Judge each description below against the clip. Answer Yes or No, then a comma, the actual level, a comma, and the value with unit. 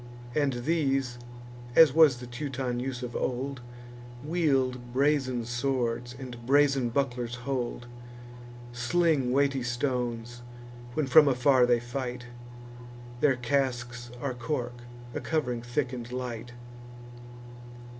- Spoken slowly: Yes, slow, 110 wpm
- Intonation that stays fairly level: Yes, narrow, 2.3 semitones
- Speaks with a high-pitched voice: No, low, 125 Hz